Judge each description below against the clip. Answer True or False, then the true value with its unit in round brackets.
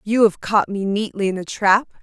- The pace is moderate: False (235 wpm)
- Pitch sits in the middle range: False (205 Hz)